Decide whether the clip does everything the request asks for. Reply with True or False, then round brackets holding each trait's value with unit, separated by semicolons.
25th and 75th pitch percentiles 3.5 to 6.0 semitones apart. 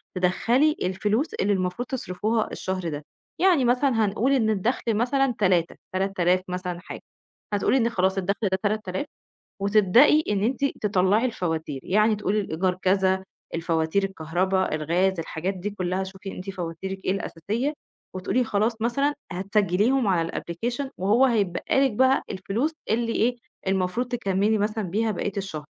True (3.9 semitones)